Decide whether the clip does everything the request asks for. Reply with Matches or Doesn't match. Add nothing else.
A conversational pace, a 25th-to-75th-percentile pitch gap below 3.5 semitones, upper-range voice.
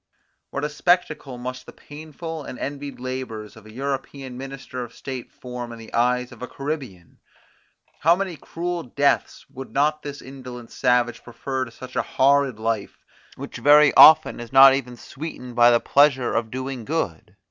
Doesn't match